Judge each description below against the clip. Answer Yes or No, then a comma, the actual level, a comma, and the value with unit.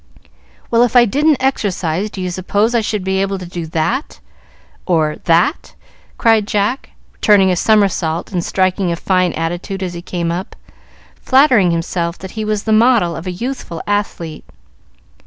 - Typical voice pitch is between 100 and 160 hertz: No, high, 190 Hz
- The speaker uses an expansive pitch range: No, average, 4.0 semitones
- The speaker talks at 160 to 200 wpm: Yes, average, 165 wpm